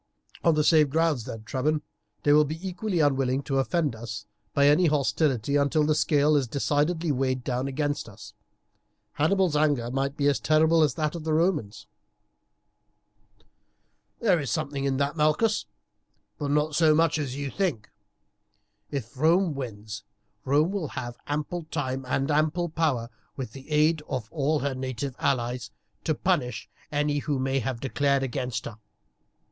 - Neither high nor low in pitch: Yes, medium, 145 Hz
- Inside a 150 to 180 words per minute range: Yes, average, 160 wpm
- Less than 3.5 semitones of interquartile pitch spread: Yes, average, 3.0 semitones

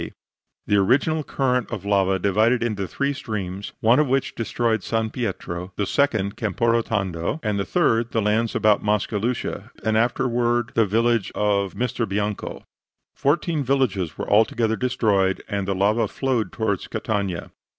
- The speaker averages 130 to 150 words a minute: Yes, average, 145 wpm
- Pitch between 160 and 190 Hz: No, low, 110 Hz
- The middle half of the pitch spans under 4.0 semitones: Yes, average, 3.2 semitones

